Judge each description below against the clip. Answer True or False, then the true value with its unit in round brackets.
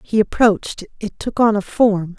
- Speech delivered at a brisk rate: False (195 wpm)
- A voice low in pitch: False (215 Hz)